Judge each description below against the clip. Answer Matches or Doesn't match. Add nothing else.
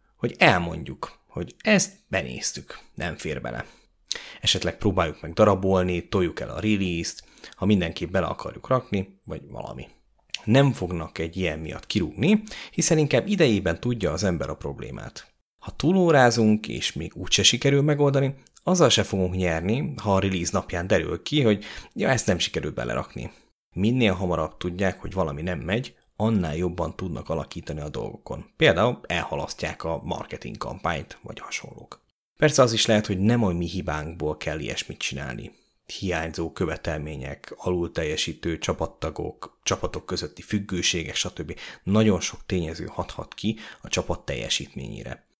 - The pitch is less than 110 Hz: Matches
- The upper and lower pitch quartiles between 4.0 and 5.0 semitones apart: Matches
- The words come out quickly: Doesn't match